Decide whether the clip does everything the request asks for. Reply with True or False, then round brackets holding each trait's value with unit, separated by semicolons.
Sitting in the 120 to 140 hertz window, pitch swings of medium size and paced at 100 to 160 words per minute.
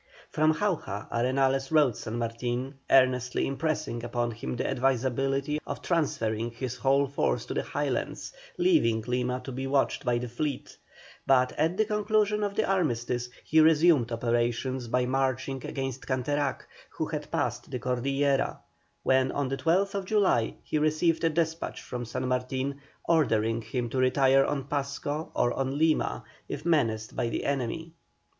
True (135 Hz; 3.7 semitones; 155 wpm)